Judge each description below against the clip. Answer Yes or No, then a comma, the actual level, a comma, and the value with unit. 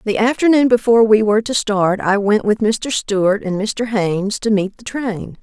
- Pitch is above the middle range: Yes, high, 215 Hz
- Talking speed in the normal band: No, fast, 210 wpm